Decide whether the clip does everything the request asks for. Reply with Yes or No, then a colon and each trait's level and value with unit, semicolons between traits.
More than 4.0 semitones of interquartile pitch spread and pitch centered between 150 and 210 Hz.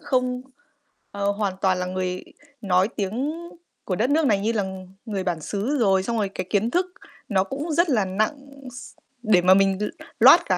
Yes: average, 4.7 semitones; high, 205 Hz